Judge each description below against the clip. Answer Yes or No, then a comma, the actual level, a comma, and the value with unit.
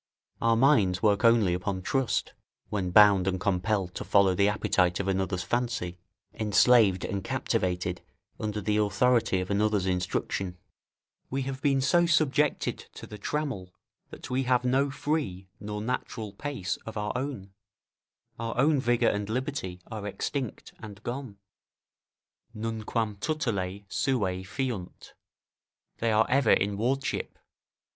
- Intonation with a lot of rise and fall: No, average, 4.8 semitones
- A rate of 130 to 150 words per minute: Yes, slow, 135 wpm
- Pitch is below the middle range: Yes, low, 105 Hz